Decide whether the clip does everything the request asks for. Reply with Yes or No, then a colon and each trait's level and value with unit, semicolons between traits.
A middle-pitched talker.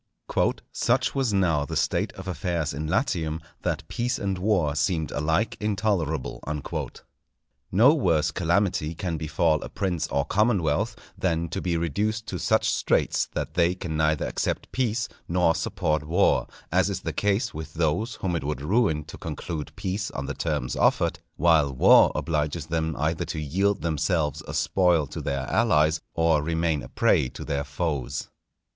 No: very low, 85 Hz